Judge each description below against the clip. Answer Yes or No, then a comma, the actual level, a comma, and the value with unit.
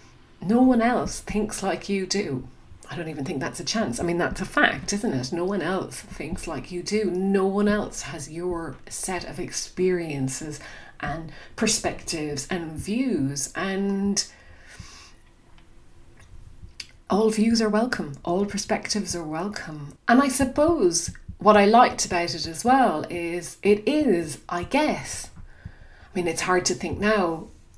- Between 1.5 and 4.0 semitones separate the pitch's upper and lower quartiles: No, average, 4.4 semitones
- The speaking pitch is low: No, high, 190 Hz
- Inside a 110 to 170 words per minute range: Yes, average, 155 wpm